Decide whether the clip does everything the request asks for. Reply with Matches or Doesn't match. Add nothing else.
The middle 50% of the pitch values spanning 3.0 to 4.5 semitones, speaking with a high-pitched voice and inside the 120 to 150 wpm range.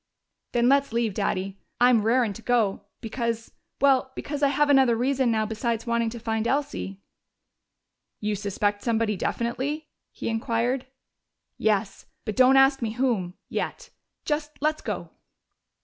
Matches